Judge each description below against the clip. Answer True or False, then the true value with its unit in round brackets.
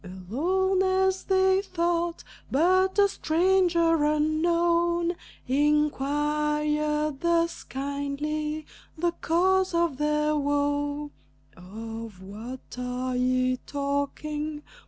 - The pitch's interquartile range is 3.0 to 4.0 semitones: True (3.4 semitones)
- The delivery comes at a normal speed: False (85 wpm)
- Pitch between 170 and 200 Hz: False (300 Hz)